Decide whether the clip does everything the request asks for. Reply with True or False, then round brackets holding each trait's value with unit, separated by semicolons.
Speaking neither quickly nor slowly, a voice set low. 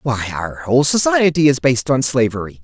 True (180 wpm; 130 Hz)